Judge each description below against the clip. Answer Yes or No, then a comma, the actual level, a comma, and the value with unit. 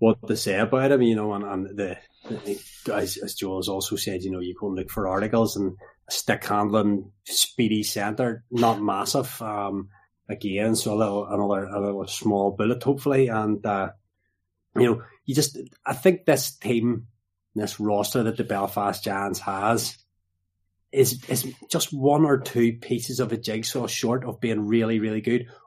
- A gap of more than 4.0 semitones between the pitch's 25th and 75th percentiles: No, average, 3.3 semitones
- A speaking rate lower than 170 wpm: No, average, 180 wpm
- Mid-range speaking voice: No, low, 110 Hz